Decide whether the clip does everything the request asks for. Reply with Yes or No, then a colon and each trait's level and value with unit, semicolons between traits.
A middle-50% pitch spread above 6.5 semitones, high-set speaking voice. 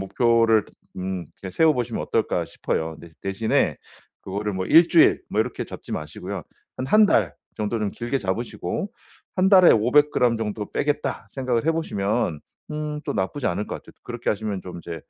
No: wide, 6.9 semitones; low, 110 Hz